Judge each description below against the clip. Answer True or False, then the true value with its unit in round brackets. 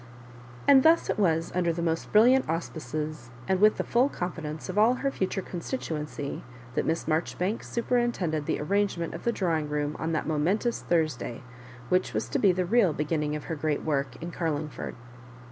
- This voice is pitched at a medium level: True (170 Hz)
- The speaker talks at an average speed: True (190 wpm)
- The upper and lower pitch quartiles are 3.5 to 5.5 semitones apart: True (5.0 semitones)